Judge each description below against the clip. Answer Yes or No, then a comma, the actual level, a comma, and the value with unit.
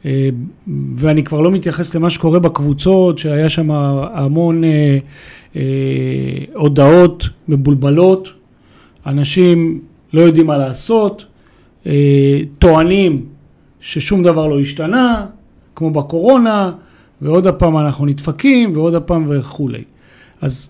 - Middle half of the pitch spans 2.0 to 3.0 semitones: No, average, 3.6 semitones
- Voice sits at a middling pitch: Yes, medium, 155 Hz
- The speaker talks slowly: Yes, slow, 95 wpm